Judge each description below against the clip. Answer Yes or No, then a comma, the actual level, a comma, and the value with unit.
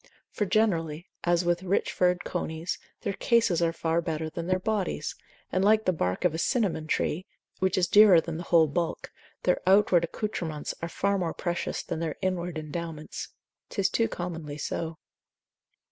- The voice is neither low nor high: Yes, medium, 175 Hz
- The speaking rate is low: No, average, 170 wpm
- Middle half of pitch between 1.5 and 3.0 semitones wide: Yes, narrow, 2.6 semitones